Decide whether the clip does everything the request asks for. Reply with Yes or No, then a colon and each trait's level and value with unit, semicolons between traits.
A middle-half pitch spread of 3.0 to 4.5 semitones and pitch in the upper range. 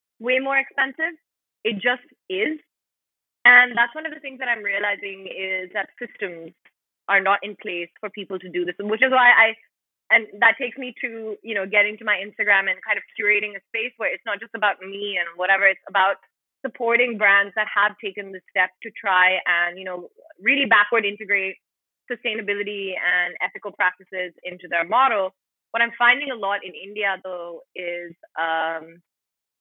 Yes: average, 4.0 semitones; high, 205 Hz